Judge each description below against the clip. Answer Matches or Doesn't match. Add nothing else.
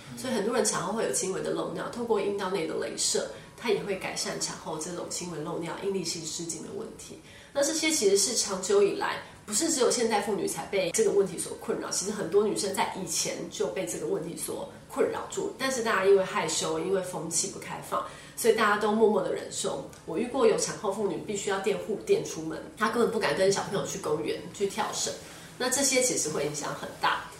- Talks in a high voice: Matches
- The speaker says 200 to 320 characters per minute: Doesn't match